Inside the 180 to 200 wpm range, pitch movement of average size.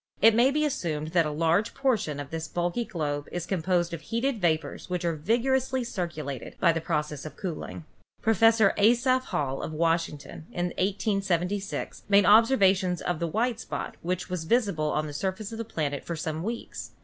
No: average, 185 wpm; wide, 5.7 semitones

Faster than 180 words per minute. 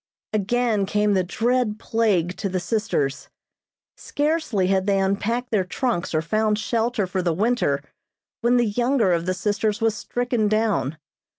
No: average, 155 wpm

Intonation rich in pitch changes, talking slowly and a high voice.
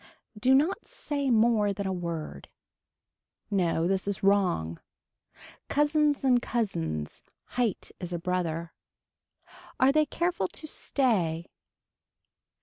Yes: wide, 7.6 semitones; slow, 110 wpm; high, 200 Hz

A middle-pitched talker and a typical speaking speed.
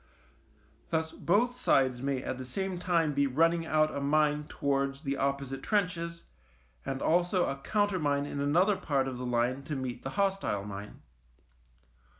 Yes: medium, 145 Hz; average, 155 wpm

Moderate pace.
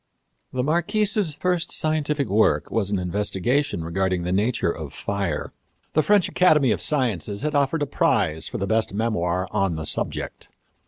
Yes: average, 160 wpm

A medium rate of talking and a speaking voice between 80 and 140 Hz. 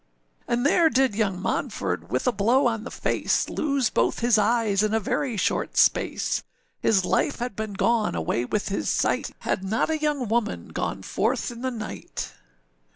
No: average, 180 wpm; high, 225 Hz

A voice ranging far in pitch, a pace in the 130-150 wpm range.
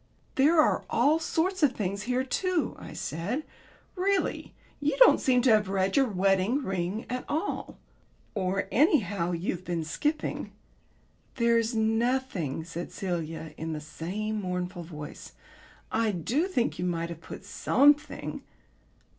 Yes: wide, 7.2 semitones; average, 140 wpm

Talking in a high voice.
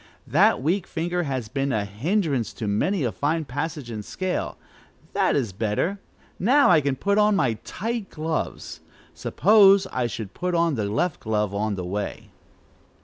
No: medium, 145 Hz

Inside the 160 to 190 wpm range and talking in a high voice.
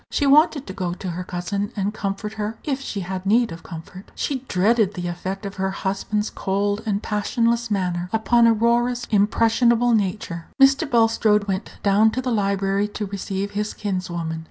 Yes: average, 175 wpm; high, 205 Hz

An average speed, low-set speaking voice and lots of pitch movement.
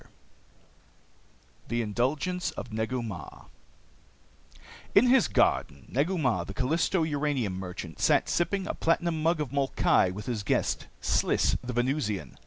Yes: average, 150 wpm; low, 130 Hz; wide, 7.3 semitones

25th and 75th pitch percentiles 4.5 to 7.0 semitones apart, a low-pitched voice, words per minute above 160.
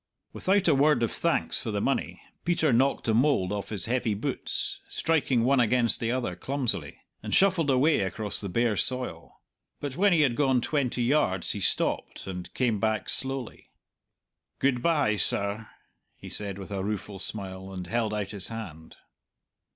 Yes: average, 5.2 semitones; low, 115 Hz; average, 170 wpm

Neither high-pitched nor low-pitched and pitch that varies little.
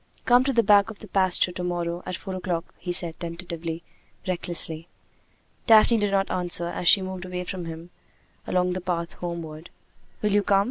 Yes: medium, 180 Hz; narrow, 2.3 semitones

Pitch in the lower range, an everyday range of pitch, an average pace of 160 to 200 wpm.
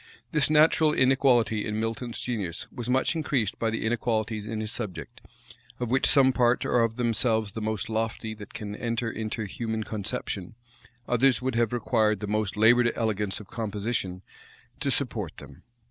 No: low, 115 Hz; narrow, 2.3 semitones; average, 165 wpm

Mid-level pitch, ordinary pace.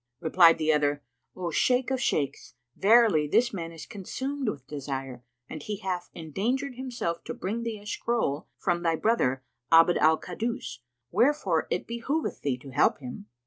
Yes: medium, 175 Hz; average, 165 wpm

